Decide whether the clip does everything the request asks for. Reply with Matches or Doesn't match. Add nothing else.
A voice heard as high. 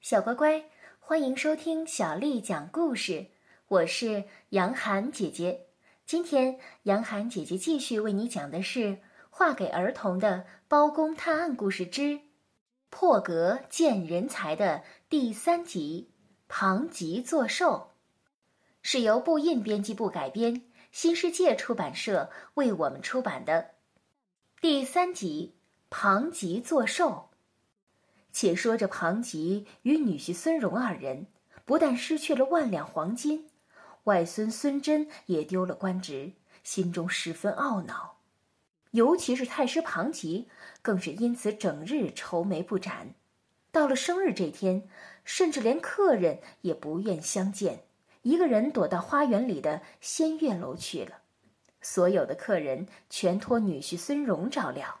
Matches